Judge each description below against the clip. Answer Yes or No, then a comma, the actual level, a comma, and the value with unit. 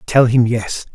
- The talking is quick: No, average, 190 wpm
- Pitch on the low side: Yes, low, 120 Hz